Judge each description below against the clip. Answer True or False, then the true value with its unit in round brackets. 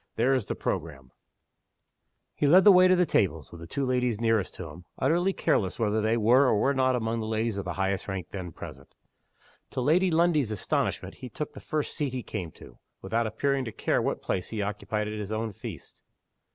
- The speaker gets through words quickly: True (215 wpm)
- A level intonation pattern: False (5.3 semitones)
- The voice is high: False (115 Hz)